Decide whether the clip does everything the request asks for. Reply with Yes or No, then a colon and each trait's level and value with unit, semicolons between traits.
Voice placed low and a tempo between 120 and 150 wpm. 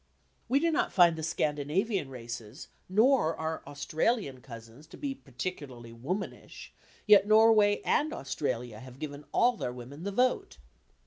No: medium, 155 Hz; average, 140 wpm